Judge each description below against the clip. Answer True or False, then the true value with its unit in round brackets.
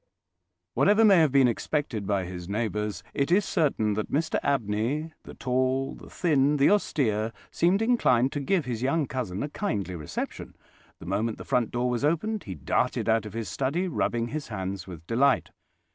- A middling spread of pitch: False (6.1 semitones)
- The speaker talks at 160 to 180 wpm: True (175 wpm)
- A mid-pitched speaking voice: False (125 Hz)